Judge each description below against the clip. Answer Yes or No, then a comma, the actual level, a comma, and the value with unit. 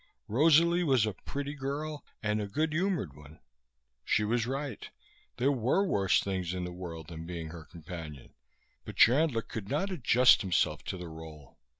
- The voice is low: Yes, low, 110 Hz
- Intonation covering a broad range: Yes, wide, 8.7 semitones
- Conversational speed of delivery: Yes, average, 170 wpm